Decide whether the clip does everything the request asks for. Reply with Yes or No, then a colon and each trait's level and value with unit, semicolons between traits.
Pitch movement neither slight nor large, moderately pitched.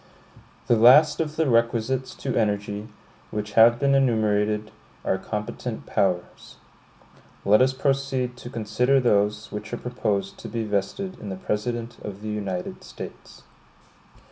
No: average, 3.3 semitones; low, 110 Hz